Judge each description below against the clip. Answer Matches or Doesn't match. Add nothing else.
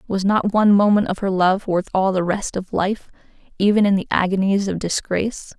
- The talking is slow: Doesn't match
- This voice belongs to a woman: Matches